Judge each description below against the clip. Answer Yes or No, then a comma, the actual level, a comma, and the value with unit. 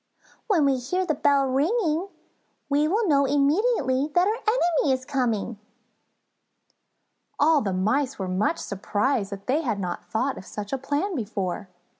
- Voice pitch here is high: Yes, very high, 275 Hz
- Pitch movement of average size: No, wide, 6.3 semitones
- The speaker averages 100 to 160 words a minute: Yes, average, 155 wpm